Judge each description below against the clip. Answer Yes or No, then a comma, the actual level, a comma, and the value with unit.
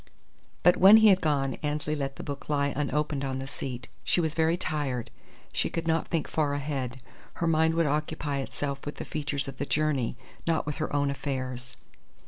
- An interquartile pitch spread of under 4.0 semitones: Yes, narrow, 2.5 semitones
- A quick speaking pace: No, average, 195 wpm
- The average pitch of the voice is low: No, medium, 145 Hz